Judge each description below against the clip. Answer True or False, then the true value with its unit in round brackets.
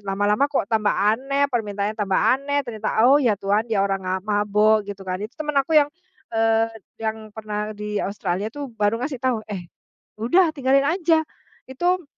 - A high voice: True (220 Hz)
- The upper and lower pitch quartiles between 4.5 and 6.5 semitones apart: True (4.8 semitones)